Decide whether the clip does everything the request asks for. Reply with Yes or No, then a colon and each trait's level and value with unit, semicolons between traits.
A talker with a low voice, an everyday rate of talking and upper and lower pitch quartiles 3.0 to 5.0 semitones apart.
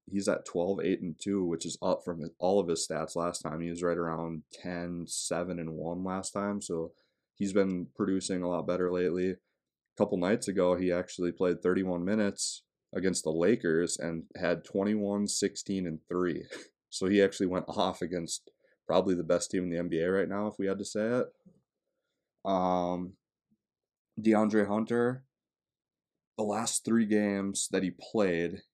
No: very low, 90 Hz; average, 175 wpm; narrow, 2.5 semitones